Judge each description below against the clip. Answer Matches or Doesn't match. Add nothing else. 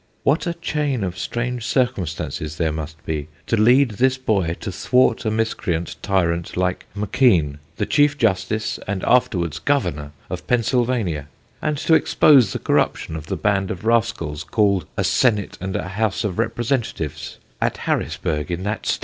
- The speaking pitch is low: Matches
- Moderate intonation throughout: Doesn't match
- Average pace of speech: Matches